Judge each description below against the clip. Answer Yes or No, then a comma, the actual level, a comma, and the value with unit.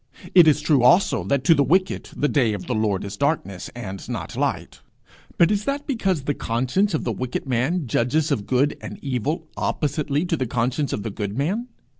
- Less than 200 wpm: No, fast, 205 wpm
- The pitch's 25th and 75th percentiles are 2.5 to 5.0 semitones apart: No, wide, 5.4 semitones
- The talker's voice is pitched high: No, medium, 140 Hz